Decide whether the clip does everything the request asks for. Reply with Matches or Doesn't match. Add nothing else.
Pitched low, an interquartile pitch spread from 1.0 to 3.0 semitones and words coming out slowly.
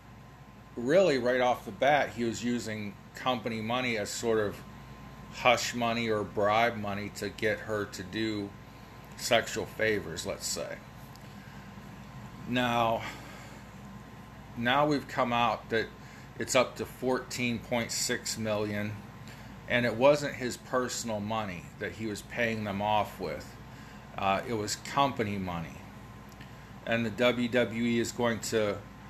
Matches